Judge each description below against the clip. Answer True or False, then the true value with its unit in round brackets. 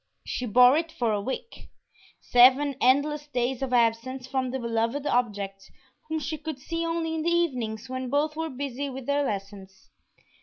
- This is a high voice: True (260 Hz)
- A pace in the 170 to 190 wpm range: True (175 wpm)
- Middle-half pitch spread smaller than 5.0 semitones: True (3.7 semitones)